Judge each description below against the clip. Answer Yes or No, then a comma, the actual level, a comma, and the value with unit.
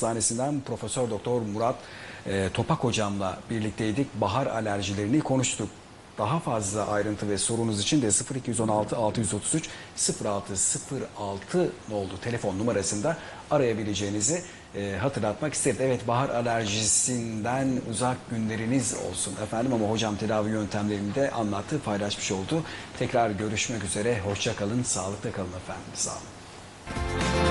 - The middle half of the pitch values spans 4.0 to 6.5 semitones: No, average, 3.1 semitones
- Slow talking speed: No, average, 115 wpm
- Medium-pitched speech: No, low, 110 Hz